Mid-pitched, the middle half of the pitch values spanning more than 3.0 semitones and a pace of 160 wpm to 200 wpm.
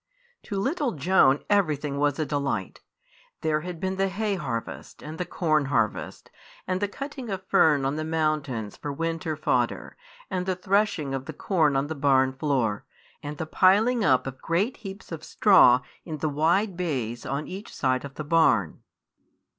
Yes: medium, 155 Hz; wide, 5.4 semitones; average, 170 wpm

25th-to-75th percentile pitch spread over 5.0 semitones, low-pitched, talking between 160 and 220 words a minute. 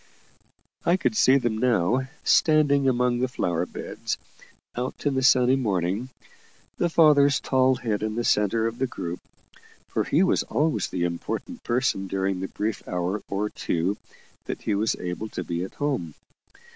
Yes: wide, 5.5 semitones; low, 120 Hz; average, 165 wpm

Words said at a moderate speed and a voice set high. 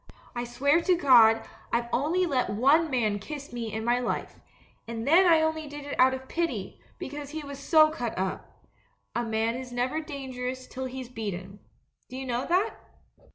Yes: average, 195 wpm; very high, 260 Hz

